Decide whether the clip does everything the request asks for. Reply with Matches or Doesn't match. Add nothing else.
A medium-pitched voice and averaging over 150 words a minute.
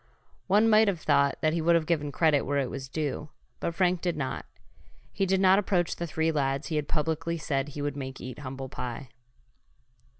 Matches